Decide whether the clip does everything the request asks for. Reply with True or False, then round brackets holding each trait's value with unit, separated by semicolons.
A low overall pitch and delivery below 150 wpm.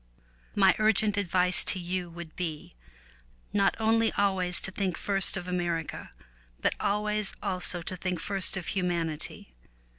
False (185 Hz; 140 wpm)